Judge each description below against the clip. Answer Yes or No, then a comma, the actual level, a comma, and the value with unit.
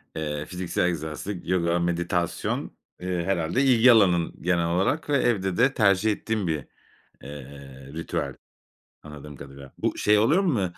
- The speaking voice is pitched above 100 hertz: No, very low, 90 Hz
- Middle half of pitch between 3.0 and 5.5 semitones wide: Yes, average, 5.1 semitones